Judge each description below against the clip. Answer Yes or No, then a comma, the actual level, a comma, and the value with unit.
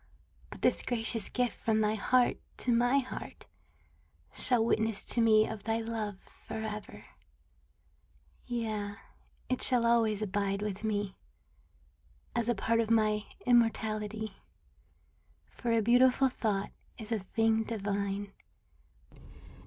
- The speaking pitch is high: Yes, high, 220 Hz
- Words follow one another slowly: Yes, slow, 120 wpm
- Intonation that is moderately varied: No, narrow, 1.9 semitones